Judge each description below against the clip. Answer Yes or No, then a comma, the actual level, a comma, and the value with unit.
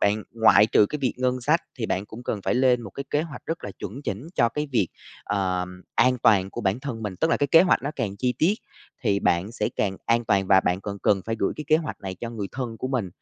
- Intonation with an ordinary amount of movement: Yes, average, 4.6 semitones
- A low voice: Yes, low, 115 Hz